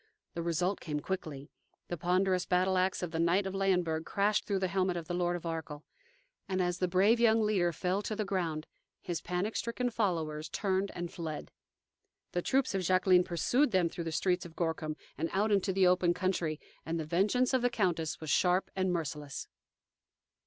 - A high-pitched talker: No, medium, 180 Hz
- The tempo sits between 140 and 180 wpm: No, average, 195 wpm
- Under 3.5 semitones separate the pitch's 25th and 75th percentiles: Yes, narrow, 2.6 semitones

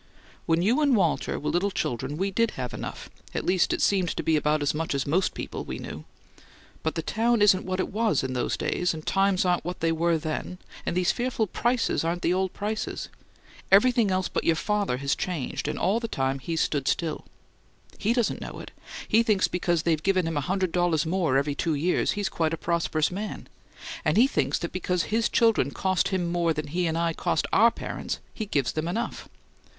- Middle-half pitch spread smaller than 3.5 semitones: No, average, 4.0 semitones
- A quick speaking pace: Yes, fast, 220 wpm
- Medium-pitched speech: Yes, medium, 175 Hz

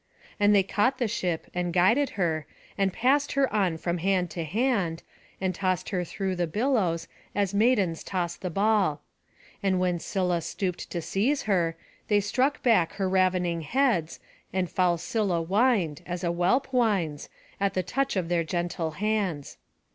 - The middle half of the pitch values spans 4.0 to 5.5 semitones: No, average, 3.5 semitones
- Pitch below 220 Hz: Yes, medium, 185 Hz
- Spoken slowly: No, average, 165 wpm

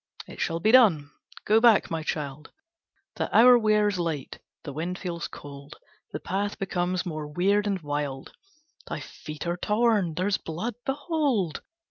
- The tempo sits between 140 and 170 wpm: Yes, average, 150 wpm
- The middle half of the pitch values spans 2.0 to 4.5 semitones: No, wide, 5.5 semitones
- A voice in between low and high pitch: Yes, medium, 180 Hz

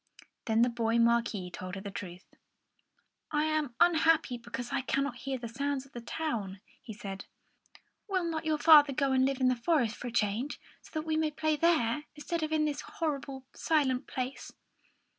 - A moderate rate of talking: Yes, average, 195 wpm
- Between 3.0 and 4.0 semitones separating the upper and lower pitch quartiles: No, average, 4.7 semitones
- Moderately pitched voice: No, very high, 265 Hz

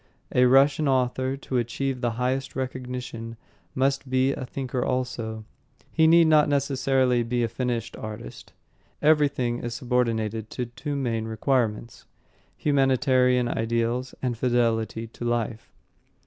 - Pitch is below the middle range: Yes, low, 125 Hz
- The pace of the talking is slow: Yes, slow, 125 wpm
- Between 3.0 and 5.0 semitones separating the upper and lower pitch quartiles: No, narrow, 2.4 semitones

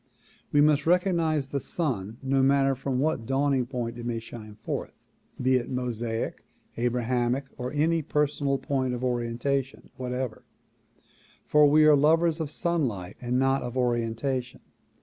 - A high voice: No, low, 130 Hz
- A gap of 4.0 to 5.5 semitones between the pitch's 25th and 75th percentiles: No, average, 3.2 semitones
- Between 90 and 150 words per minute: Yes, average, 145 wpm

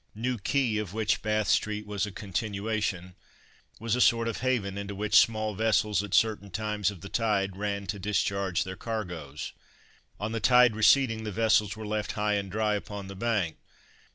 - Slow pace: No, average, 180 wpm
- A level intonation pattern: Yes, narrow, 1.9 semitones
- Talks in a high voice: No, low, 105 Hz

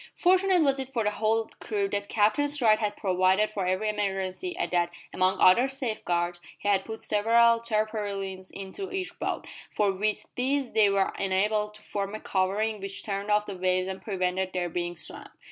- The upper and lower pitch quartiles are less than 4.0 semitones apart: Yes, average, 2.9 semitones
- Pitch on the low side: No, high, 205 Hz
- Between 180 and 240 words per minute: Yes, average, 185 wpm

